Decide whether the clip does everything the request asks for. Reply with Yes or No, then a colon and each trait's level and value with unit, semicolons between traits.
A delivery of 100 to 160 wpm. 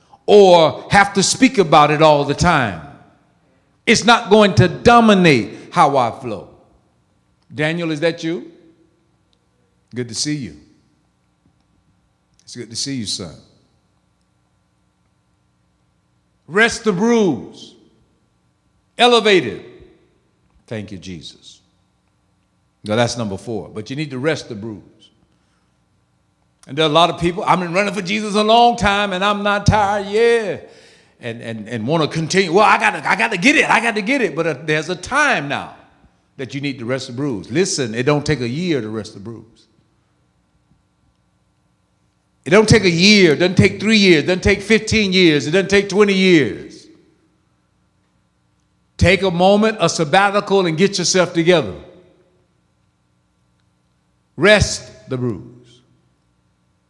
Yes: average, 150 wpm